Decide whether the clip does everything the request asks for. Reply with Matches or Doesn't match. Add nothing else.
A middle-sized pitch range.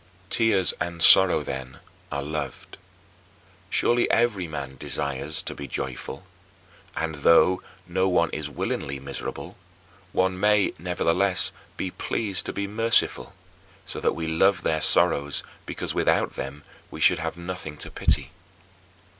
Matches